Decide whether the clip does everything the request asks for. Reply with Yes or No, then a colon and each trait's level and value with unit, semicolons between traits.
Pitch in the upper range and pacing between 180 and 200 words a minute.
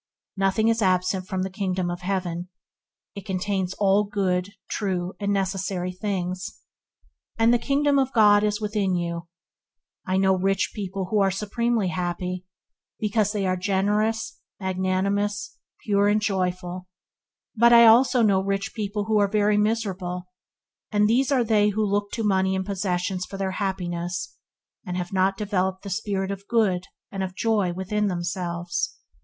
No: high, 195 Hz; average, 155 wpm